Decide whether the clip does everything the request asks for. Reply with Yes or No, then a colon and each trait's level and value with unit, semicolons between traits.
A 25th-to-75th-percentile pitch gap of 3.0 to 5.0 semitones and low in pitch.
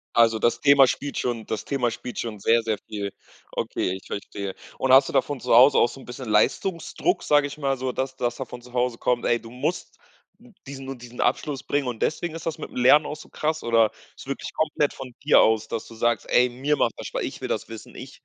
Yes: average, 3.4 semitones; low, 125 Hz